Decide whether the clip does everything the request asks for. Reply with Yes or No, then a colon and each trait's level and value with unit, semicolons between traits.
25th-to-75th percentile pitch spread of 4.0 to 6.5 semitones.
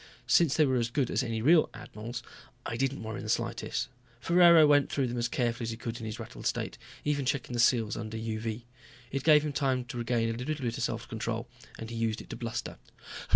No: average, 3.2 semitones